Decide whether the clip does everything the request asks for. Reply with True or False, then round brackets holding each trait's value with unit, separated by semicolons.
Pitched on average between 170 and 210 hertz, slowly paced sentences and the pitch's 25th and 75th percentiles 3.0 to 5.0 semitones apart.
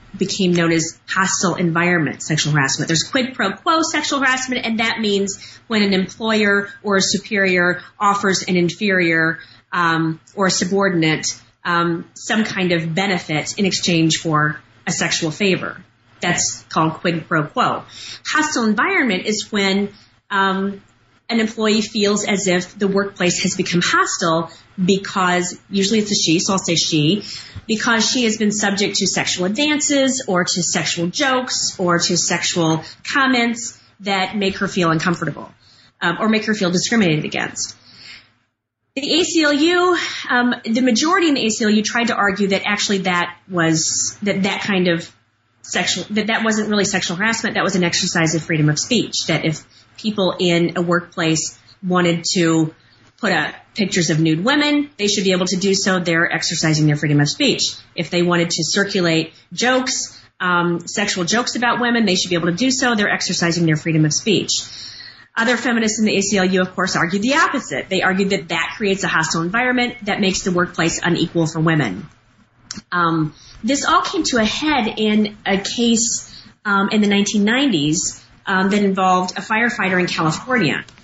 False (190 Hz; 170 wpm; 4.2 semitones)